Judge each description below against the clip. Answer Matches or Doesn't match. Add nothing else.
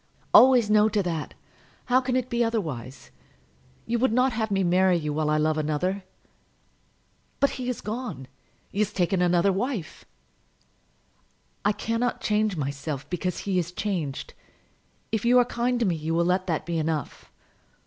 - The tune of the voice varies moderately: Doesn't match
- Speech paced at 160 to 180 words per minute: Matches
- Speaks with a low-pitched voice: Doesn't match